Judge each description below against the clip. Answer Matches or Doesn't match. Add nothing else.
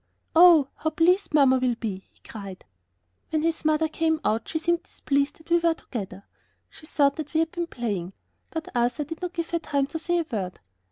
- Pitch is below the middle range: Doesn't match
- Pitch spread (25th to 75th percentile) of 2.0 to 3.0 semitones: Doesn't match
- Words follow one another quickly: Matches